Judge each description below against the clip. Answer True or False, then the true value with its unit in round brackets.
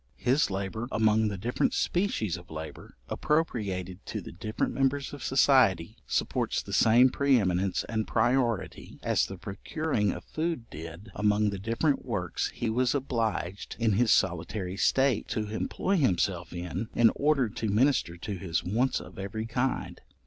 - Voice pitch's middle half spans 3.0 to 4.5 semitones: False (5.3 semitones)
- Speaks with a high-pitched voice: False (110 Hz)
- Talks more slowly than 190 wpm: True (155 wpm)